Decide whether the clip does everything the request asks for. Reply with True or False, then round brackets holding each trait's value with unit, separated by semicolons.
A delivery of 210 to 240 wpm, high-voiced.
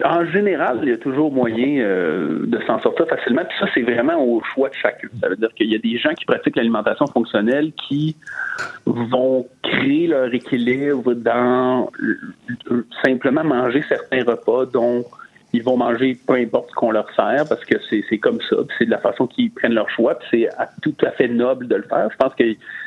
False (215 wpm; 125 Hz)